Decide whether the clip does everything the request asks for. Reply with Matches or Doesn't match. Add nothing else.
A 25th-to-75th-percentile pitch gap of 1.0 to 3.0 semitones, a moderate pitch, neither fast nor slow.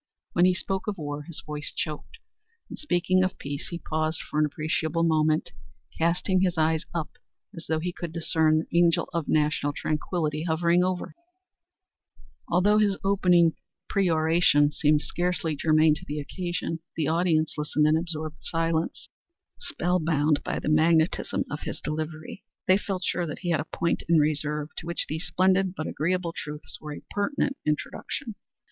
Matches